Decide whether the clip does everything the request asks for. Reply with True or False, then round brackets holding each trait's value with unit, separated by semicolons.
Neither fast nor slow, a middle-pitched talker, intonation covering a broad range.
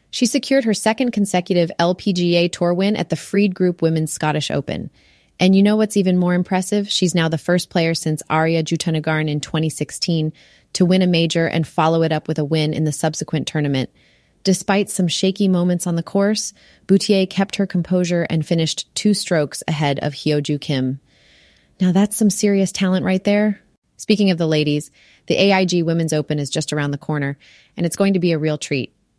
False (195 wpm; 170 Hz; 3.7 semitones)